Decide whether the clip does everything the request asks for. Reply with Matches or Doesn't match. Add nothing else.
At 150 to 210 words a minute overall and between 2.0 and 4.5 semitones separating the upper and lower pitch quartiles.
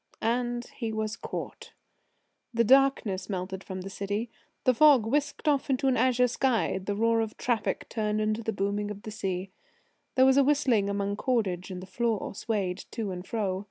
Matches